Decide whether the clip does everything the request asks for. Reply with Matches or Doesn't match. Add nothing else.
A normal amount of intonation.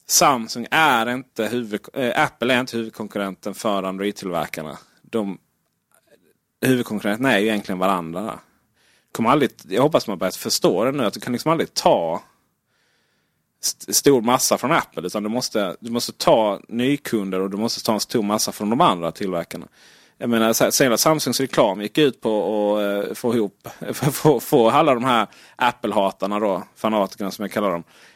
Matches